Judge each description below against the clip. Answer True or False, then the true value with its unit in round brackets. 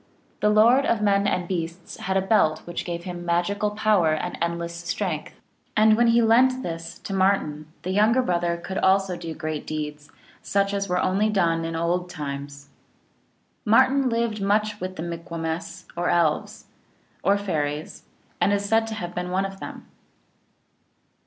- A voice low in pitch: False (185 Hz)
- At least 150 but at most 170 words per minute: True (165 wpm)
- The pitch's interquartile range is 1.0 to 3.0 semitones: False (3.8 semitones)